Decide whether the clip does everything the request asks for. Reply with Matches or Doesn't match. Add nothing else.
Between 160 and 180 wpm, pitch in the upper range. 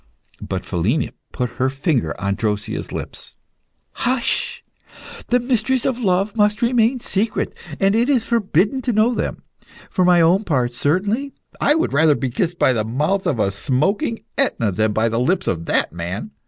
Doesn't match